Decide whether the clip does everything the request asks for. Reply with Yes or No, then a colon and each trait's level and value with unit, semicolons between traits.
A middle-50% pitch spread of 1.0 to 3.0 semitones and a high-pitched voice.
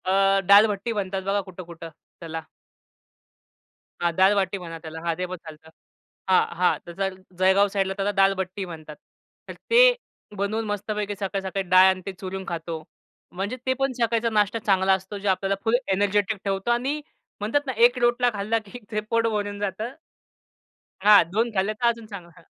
Yes: narrow, 2.4 semitones; high, 195 Hz